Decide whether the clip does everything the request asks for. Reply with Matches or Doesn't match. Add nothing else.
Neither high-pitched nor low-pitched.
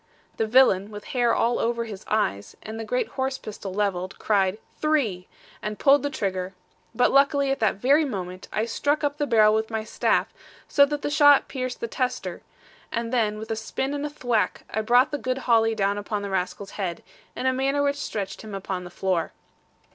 Doesn't match